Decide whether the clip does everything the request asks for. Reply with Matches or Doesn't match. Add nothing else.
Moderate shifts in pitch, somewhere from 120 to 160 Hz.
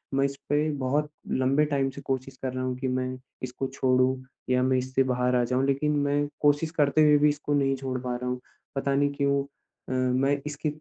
Doesn't match